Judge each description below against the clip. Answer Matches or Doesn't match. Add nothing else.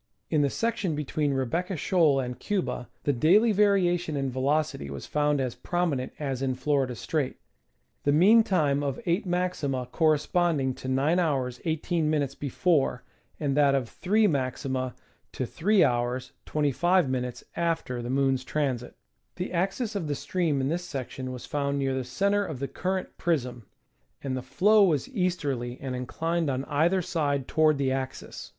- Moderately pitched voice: Matches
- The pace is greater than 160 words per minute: Doesn't match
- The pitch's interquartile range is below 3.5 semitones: Doesn't match